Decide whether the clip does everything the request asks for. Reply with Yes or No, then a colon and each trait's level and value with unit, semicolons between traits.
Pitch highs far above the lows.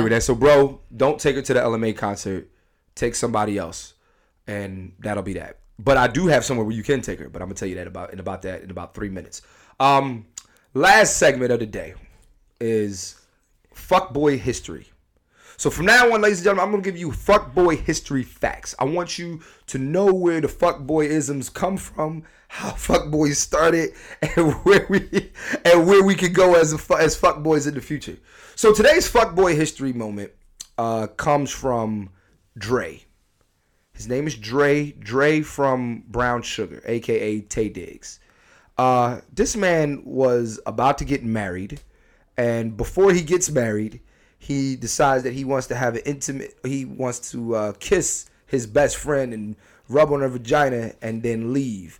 Yes: wide, 6.2 semitones